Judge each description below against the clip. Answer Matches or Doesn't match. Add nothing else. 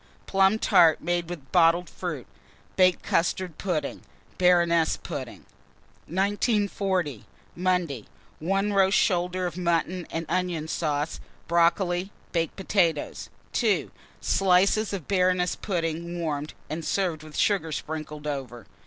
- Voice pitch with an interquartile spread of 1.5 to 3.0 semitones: Matches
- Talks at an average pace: Doesn't match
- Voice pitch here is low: Doesn't match